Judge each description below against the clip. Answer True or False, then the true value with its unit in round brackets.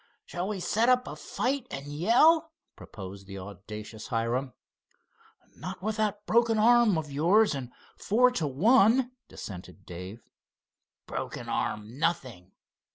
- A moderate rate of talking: False (130 wpm)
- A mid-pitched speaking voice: True (165 Hz)